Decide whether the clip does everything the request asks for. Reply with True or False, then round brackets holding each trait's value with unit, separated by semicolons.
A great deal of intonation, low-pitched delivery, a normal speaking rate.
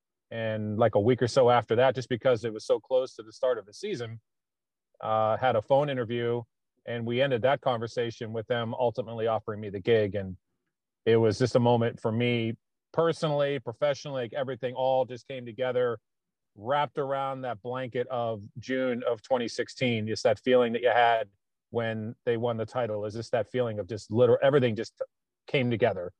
False (2.4 semitones; 120 Hz; 190 wpm)